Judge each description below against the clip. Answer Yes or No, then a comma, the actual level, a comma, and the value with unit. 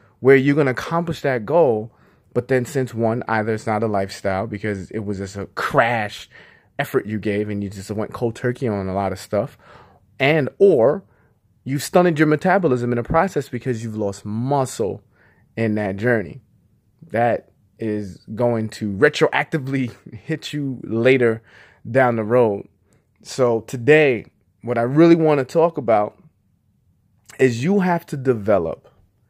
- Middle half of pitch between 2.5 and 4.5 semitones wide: No, average, 5.1 semitones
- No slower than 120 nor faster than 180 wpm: Yes, average, 160 wpm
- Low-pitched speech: Yes, low, 120 Hz